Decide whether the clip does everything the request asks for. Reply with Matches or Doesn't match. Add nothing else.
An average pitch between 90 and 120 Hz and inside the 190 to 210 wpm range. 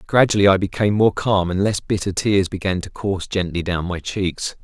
Matches